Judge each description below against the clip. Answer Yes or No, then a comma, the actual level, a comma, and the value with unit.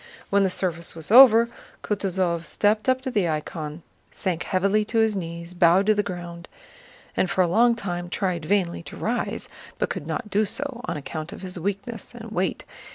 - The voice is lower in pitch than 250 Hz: Yes, high, 190 Hz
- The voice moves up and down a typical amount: Yes, average, 4.0 semitones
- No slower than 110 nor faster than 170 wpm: No, average, 190 wpm